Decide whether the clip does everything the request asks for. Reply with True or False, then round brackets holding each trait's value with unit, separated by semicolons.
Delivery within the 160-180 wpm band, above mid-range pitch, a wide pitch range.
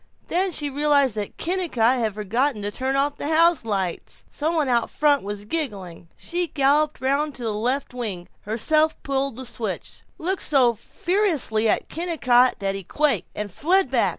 True (170 wpm; 270 Hz; 5.9 semitones)